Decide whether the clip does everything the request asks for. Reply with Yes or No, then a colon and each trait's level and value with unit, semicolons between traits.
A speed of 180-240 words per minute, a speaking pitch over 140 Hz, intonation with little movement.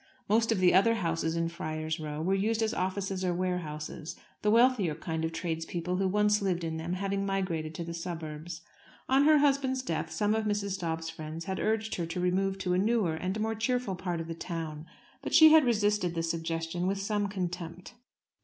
No: average, 200 wpm; medium, 185 Hz; average, 4.0 semitones